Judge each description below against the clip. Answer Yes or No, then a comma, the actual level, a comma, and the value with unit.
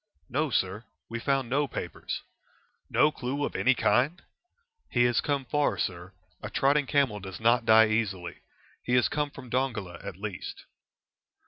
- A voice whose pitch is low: Yes, low, 120 Hz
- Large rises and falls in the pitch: No, average, 4.7 semitones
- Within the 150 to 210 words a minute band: Yes, average, 155 wpm